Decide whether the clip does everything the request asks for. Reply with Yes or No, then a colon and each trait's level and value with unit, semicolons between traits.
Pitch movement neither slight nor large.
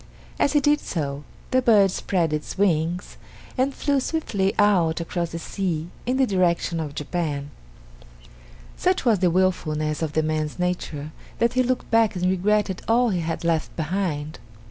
Yes: average, 5.0 semitones